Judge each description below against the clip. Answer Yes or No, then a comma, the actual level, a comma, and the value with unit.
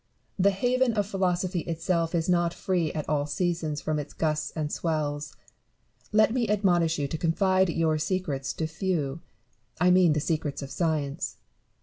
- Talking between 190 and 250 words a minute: No, average, 160 wpm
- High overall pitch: No, medium, 165 Hz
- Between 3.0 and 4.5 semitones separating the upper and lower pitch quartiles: Yes, average, 3.4 semitones